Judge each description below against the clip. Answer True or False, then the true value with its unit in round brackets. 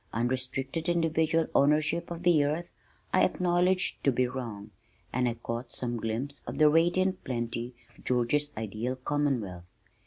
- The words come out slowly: False (145 wpm)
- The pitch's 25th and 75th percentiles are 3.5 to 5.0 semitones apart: False (5.4 semitones)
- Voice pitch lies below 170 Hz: True (135 Hz)